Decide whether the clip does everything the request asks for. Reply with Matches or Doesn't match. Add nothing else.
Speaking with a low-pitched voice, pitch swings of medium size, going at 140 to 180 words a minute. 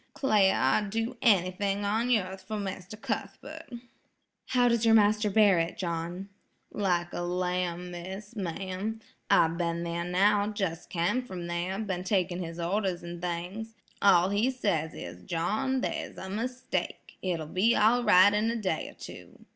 Doesn't match